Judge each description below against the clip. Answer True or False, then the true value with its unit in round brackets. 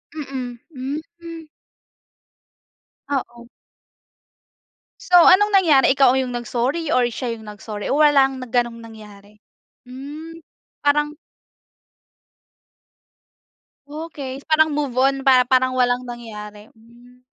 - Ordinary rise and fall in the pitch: True (3.4 semitones)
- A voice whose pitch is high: True (255 Hz)